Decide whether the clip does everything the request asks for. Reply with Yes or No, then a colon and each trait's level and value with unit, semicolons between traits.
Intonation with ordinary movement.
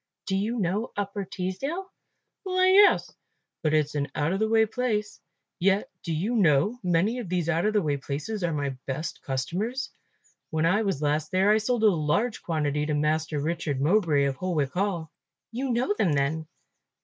No: wide, 6.1 semitones